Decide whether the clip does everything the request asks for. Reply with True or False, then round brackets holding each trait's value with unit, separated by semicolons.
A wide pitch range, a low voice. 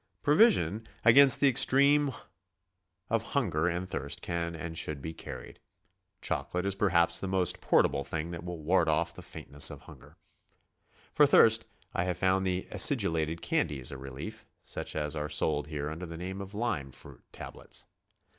False (4.2 semitones; 85 Hz)